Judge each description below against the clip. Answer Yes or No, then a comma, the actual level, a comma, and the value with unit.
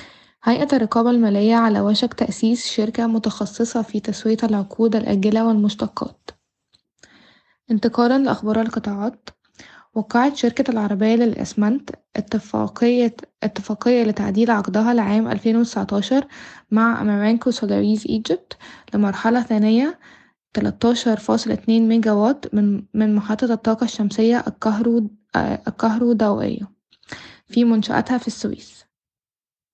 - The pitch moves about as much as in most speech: No, narrow, 1.8 semitones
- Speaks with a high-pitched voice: Yes, high, 225 Hz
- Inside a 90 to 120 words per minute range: Yes, average, 95 wpm